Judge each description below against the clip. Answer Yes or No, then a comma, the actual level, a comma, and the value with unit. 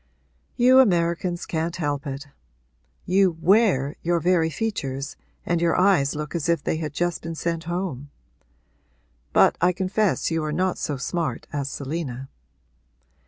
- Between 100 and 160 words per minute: Yes, average, 145 wpm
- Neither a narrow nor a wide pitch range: Yes, average, 3.6 semitones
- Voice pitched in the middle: Yes, medium, 170 Hz